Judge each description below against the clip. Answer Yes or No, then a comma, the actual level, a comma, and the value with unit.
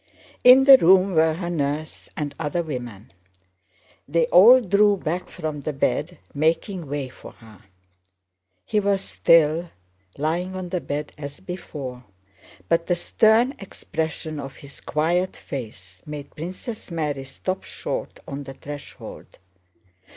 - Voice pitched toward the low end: No, medium, 160 Hz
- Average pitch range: Yes, average, 4.5 semitones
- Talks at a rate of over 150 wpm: No, slow, 135 wpm